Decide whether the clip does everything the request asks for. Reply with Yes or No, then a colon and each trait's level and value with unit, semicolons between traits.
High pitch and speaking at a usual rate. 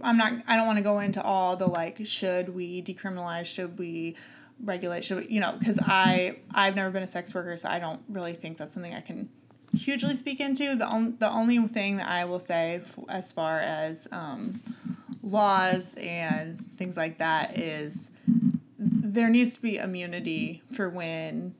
Yes: high, 195 Hz; average, 190 wpm